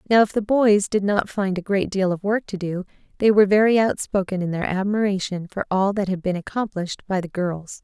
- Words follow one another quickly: Yes, fast, 230 wpm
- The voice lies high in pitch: Yes, high, 195 Hz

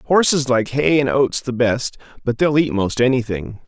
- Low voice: Yes, low, 125 Hz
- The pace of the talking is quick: No, average, 195 wpm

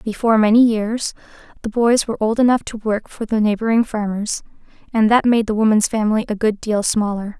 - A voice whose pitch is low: No, high, 220 Hz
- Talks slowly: No, average, 195 wpm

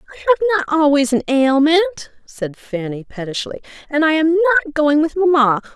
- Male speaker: No, female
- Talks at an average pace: Yes, average, 165 wpm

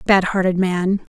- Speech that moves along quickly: No, average, 155 wpm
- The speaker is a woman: Yes, female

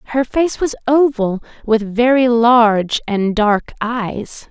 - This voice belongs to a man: No, female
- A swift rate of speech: No, slow, 135 wpm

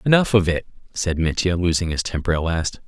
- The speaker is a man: Yes, male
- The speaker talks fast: Yes, fast, 210 wpm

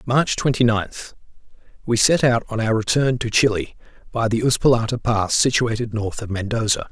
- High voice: No, low, 115 Hz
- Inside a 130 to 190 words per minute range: Yes, average, 155 wpm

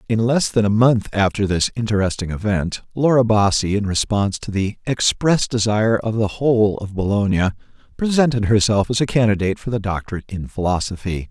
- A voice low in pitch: Yes, low, 105 Hz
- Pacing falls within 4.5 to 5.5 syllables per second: No, 5.8 syllables/s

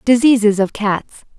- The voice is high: Yes, high, 220 Hz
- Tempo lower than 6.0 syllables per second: Yes, 4.2 syllables/s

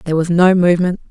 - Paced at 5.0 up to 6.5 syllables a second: No, 7.9 syllables/s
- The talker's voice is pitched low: No, medium, 175 Hz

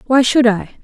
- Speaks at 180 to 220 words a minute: Yes, fast, 215 wpm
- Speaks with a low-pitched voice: No, high, 240 Hz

